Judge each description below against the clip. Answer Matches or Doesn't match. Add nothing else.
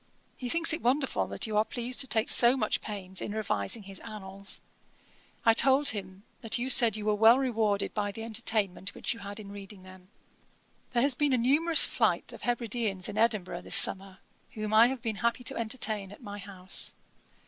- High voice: Matches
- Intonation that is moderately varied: Matches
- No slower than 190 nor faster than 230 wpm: Matches